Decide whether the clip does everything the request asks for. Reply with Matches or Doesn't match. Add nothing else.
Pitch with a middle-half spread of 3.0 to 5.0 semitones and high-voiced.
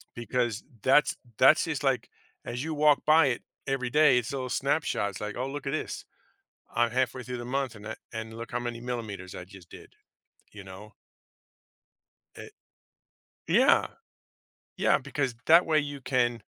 Doesn't match